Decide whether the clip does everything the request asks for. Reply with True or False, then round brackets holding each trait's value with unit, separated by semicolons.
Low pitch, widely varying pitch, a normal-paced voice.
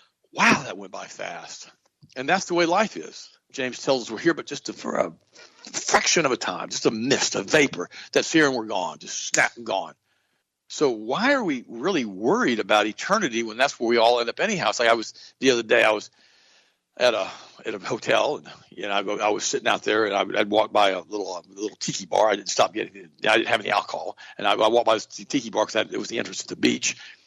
False (120 Hz; 7.1 semitones; 250 wpm)